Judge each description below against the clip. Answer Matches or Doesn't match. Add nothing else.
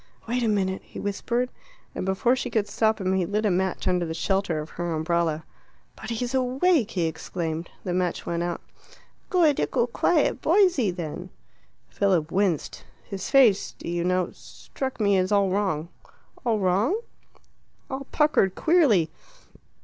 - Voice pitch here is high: Matches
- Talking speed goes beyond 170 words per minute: Doesn't match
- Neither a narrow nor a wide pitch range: Doesn't match